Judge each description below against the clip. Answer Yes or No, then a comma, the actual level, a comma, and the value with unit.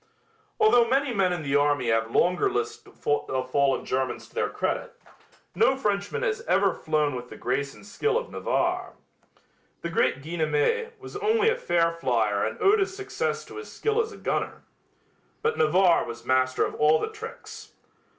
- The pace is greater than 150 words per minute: Yes, average, 175 wpm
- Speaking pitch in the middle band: Yes, medium, 180 Hz